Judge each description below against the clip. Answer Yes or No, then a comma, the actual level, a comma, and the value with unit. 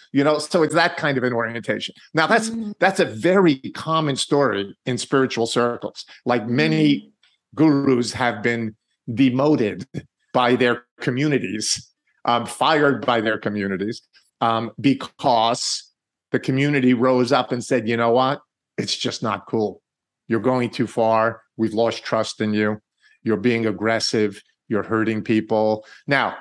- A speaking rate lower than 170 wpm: Yes, average, 145 wpm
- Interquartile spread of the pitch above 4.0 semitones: No, average, 3.6 semitones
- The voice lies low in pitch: Yes, low, 120 Hz